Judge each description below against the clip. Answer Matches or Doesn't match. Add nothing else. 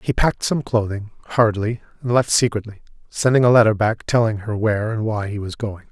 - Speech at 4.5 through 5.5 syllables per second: Doesn't match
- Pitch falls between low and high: Doesn't match